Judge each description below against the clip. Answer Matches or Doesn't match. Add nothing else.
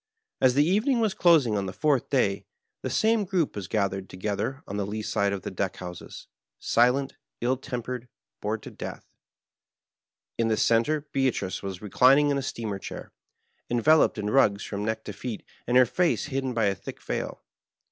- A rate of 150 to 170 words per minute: Doesn't match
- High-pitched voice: Doesn't match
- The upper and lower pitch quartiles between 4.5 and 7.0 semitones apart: Matches